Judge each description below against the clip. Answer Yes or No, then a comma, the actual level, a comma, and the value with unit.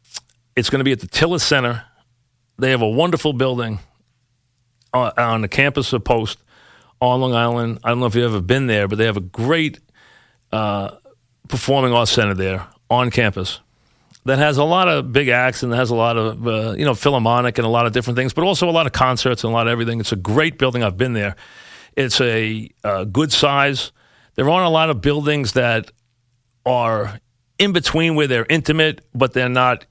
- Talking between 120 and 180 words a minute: No, fast, 205 wpm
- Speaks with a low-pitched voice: Yes, low, 125 Hz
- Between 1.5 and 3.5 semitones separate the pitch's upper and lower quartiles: Yes, average, 3.0 semitones